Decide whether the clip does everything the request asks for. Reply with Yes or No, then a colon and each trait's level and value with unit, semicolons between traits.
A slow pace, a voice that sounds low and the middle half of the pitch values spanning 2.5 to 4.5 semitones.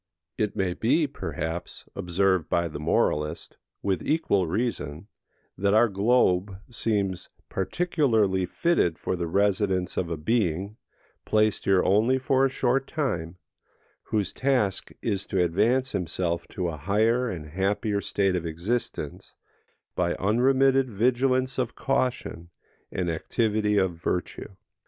No: slow, 130 wpm; low, 100 Hz; average, 5.3 semitones